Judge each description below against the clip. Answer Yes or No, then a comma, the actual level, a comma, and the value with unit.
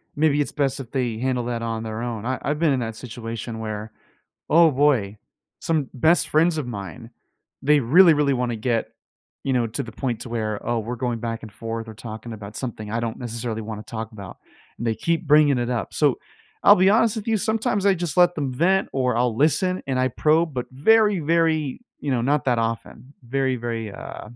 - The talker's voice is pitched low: Yes, low, 125 Hz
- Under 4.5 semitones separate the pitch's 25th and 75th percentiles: No, average, 4.8 semitones